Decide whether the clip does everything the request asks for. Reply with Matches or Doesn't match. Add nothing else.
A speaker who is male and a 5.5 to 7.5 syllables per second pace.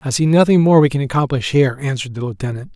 Matches